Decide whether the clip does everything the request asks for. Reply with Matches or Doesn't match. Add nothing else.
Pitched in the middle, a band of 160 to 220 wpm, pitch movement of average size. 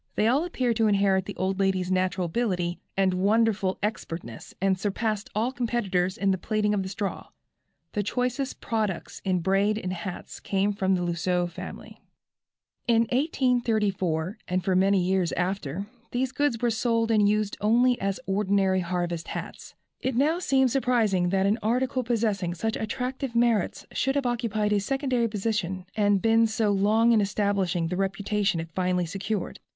Doesn't match